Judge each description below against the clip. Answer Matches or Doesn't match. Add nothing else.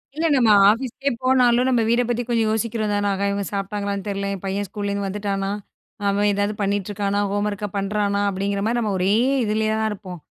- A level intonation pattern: Matches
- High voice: Matches